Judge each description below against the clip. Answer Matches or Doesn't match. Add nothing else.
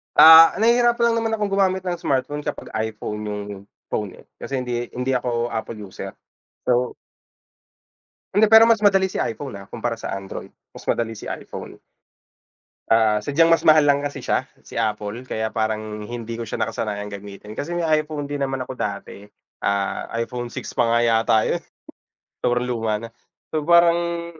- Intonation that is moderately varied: Doesn't match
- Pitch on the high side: Doesn't match